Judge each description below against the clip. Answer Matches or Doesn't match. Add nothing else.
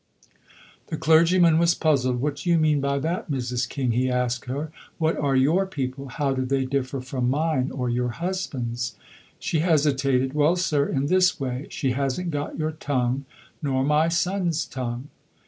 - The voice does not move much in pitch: Doesn't match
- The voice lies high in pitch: Doesn't match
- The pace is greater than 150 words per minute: Matches